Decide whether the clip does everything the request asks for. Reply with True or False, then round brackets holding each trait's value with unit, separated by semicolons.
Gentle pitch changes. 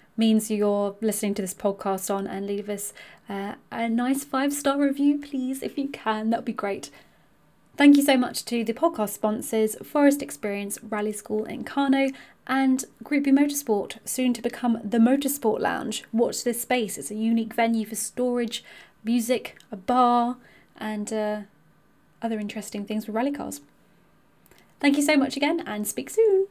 False (4.1 semitones)